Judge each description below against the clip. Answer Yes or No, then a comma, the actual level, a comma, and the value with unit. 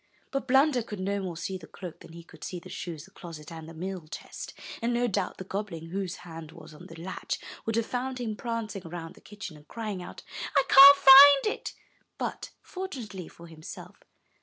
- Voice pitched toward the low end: No, high, 190 Hz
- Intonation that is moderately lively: No, wide, 6.2 semitones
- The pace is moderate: No, fast, 210 wpm